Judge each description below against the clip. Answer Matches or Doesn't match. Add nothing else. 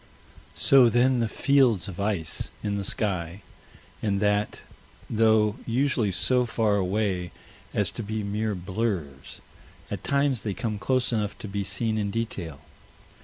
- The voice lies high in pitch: Doesn't match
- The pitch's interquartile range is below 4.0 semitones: Matches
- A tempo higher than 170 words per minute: Doesn't match